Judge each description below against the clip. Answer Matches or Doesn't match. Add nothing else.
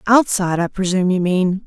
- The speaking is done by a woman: Matches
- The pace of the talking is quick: Doesn't match